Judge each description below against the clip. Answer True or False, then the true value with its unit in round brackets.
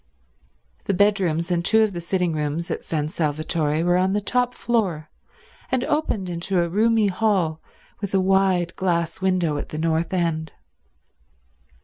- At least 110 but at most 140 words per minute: False (155 wpm)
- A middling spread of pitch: True (3.2 semitones)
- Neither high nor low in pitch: True (180 Hz)